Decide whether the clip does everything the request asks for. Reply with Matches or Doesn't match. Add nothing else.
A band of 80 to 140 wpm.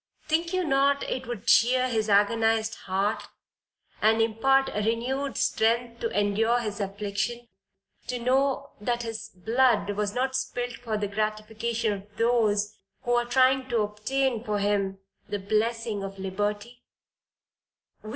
Matches